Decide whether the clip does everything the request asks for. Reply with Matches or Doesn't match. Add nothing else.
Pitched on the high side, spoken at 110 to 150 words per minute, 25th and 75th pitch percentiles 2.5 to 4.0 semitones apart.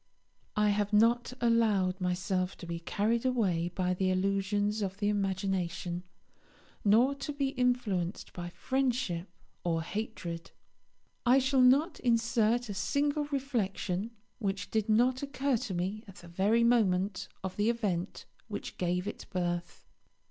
Doesn't match